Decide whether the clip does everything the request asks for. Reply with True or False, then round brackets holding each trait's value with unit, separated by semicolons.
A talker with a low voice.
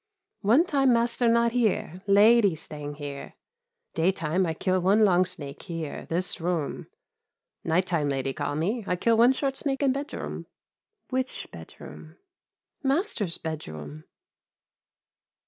False (185 Hz)